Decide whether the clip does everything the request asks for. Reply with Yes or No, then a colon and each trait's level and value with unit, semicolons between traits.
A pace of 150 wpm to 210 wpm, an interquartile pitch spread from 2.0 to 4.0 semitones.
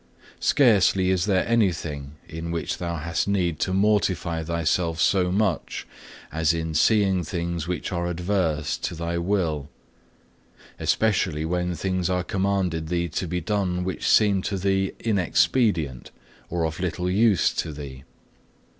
No: average, 140 wpm; average, 2.8 semitones